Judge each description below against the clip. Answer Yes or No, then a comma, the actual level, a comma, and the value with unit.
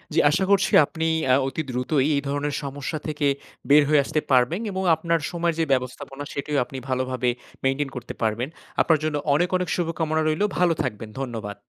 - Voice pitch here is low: No, medium, 145 Hz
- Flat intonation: No, average, 3.9 semitones